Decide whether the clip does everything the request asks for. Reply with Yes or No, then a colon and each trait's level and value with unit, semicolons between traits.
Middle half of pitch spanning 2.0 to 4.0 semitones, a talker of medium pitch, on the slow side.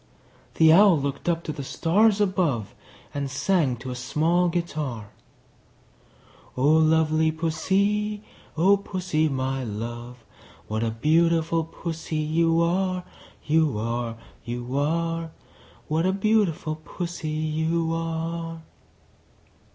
Yes: average, 3.3 semitones; medium, 160 Hz; slow, 110 wpm